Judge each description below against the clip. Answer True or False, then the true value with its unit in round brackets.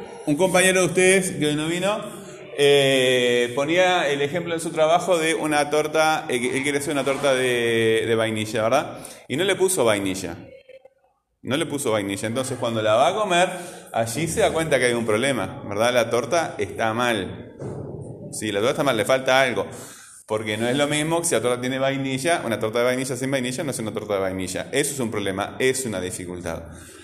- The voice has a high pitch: False (135 Hz)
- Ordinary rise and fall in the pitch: False (6.0 semitones)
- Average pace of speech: False (205 wpm)